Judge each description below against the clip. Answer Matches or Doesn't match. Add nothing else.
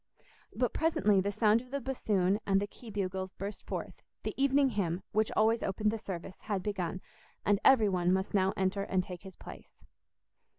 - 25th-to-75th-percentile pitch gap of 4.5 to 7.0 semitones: Doesn't match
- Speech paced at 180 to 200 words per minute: Matches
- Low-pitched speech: Doesn't match